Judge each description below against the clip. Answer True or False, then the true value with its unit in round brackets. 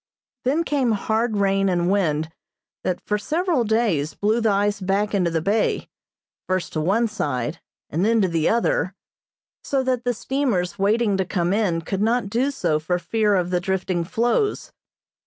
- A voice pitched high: True (200 Hz)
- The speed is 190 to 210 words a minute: False (175 wpm)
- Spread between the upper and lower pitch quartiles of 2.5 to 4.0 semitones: False (4.4 semitones)